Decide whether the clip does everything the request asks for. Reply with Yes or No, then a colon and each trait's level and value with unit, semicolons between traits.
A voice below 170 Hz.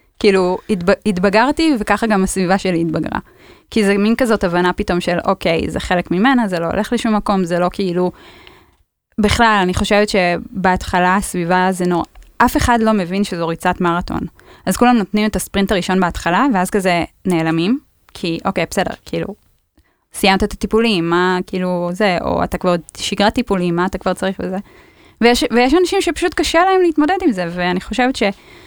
No: high, 195 Hz